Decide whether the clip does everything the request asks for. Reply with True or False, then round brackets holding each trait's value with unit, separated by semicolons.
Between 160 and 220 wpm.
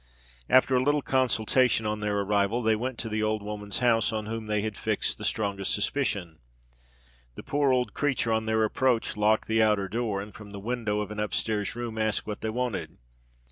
True (200 wpm)